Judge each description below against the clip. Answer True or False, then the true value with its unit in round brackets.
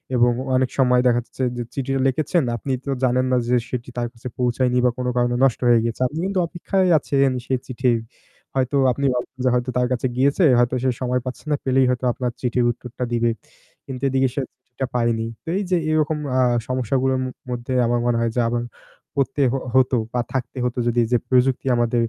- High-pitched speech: False (125 Hz)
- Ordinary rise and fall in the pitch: False (1.6 semitones)